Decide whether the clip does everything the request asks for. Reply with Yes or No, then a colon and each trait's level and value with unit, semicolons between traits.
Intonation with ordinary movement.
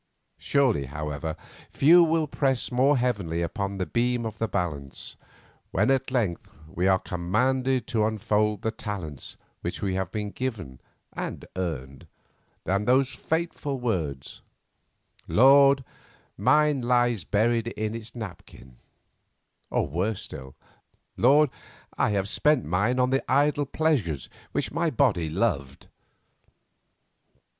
No: wide, 6.7 semitones